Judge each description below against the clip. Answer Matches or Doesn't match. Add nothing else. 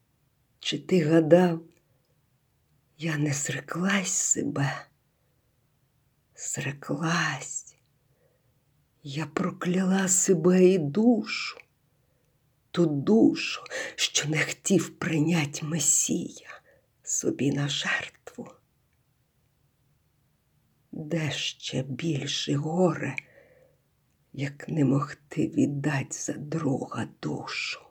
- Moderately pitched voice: Matches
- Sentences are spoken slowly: Matches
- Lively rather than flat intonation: Doesn't match